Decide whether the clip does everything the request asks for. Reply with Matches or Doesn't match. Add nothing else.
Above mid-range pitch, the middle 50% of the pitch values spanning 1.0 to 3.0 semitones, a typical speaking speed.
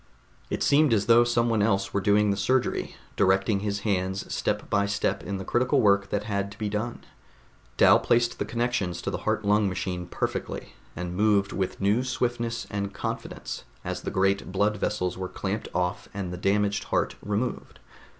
Doesn't match